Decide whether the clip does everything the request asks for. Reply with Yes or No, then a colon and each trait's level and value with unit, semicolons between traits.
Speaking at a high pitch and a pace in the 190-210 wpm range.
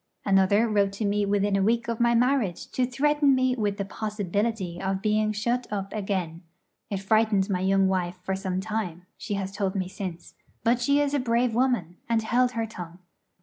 Yes: high, 210 Hz; average, 195 wpm